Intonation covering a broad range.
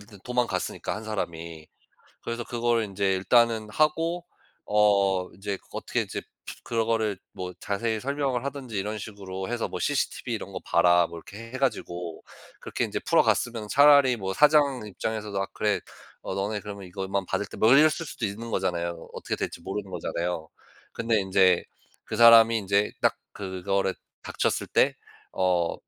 No: average, 3.7 semitones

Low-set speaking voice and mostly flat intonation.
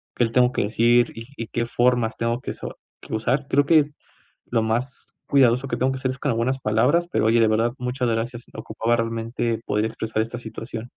Yes: low, 120 Hz; narrow, 2.0 semitones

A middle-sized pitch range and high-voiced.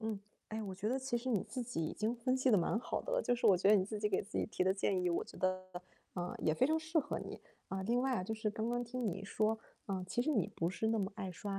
Yes: average, 4.3 semitones; high, 215 Hz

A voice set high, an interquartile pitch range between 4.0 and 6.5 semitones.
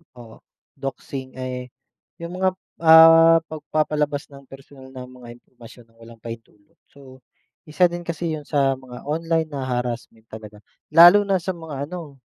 No: medium, 140 Hz; average, 4.6 semitones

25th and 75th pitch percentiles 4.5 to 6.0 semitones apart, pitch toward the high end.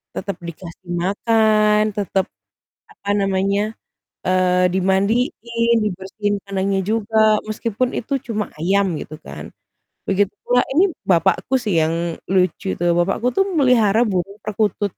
No: average, 2.7 semitones; high, 200 Hz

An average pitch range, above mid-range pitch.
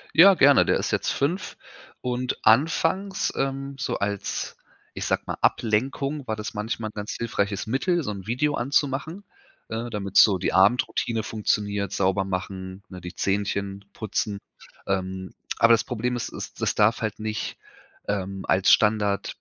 No: average, 4.7 semitones; low, 110 Hz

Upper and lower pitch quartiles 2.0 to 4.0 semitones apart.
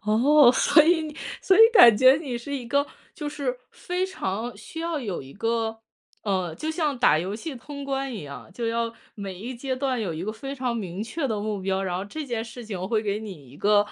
No: wide, 5.5 semitones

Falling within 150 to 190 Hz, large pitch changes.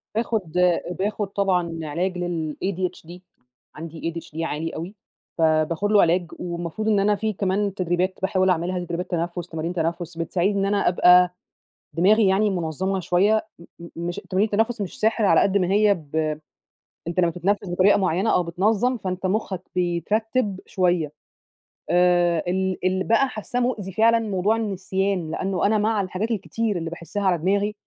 No: medium, 185 Hz; average, 3.0 semitones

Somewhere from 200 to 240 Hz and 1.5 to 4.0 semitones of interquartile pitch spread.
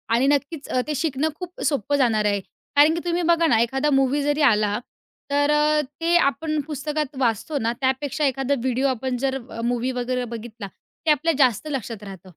No: very high, 270 Hz; average, 3.7 semitones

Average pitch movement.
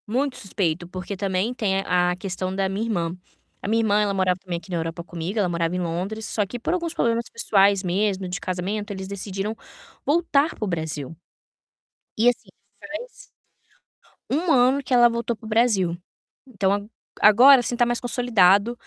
Yes: average, 4.7 semitones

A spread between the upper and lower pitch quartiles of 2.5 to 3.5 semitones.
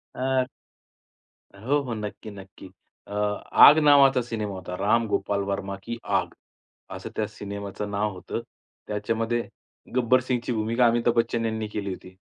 Yes: average, 2.8 semitones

